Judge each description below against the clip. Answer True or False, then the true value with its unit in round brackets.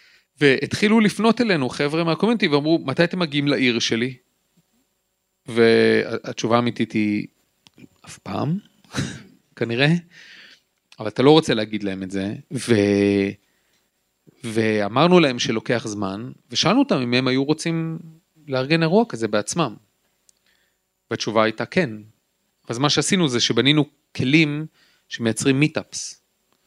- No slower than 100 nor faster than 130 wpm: True (115 wpm)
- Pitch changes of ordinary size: False (6.4 semitones)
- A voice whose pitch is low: True (130 Hz)